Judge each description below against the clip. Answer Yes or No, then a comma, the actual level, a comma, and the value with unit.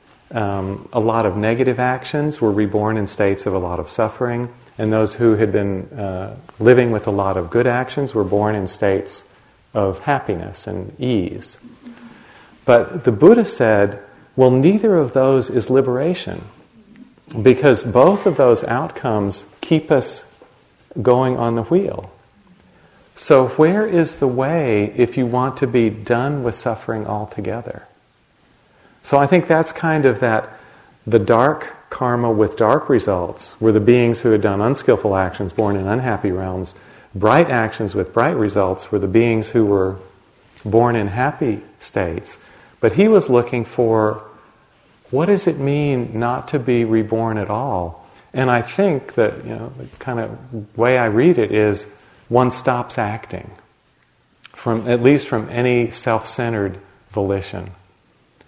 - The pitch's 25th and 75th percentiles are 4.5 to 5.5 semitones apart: No, average, 3.7 semitones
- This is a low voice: Yes, low, 115 Hz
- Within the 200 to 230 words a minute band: No, average, 155 wpm